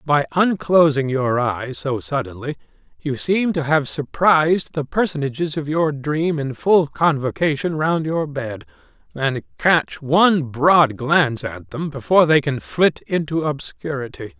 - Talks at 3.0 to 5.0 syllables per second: Yes, 4.2 syllables/s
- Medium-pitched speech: Yes, medium, 150 Hz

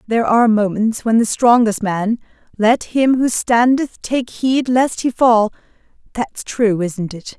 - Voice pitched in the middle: No, high, 230 Hz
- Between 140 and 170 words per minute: Yes, average, 155 wpm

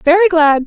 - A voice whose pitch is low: No, very high, 325 Hz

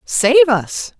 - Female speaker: Yes, female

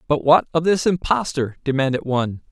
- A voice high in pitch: No, medium, 145 Hz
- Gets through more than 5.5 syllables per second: Yes, 5.7 syllables/s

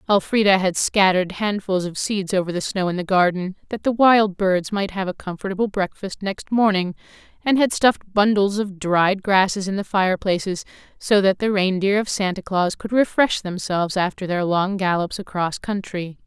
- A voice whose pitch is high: Yes, high, 195 Hz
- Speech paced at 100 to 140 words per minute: No, average, 180 wpm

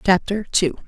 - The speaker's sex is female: Yes, female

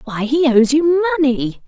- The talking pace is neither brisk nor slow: Yes, average, 180 wpm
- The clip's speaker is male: No, female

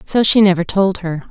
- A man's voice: No, female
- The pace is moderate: No, fast, 230 wpm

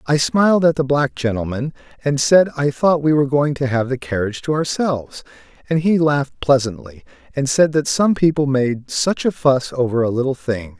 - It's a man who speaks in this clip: Yes, male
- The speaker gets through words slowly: No, average, 200 wpm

